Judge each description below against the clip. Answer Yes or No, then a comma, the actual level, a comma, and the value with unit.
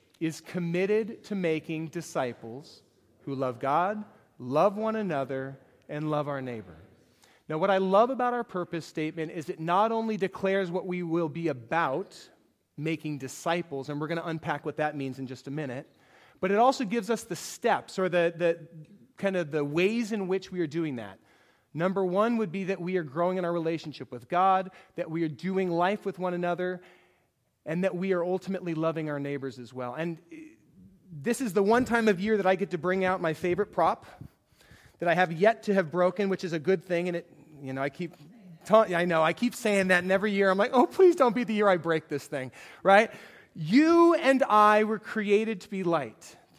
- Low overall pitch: No, medium, 175 Hz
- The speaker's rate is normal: No, fast, 210 wpm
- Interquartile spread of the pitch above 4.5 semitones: No, average, 4.2 semitones